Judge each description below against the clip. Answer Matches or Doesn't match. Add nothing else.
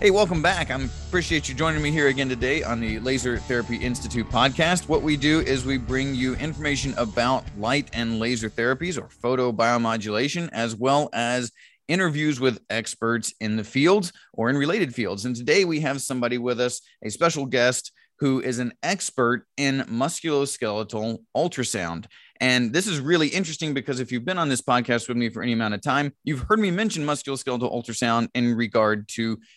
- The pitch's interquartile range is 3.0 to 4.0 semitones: Matches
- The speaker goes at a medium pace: Matches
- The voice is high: Doesn't match